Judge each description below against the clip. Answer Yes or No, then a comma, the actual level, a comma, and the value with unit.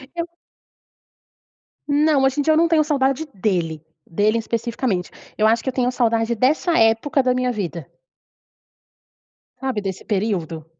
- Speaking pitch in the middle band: No, high, 235 Hz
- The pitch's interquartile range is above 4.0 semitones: Yes, average, 4.8 semitones